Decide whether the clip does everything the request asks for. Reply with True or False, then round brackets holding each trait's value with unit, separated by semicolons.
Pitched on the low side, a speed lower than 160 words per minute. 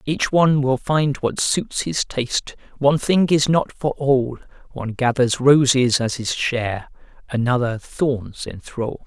True (130 Hz; 150 wpm)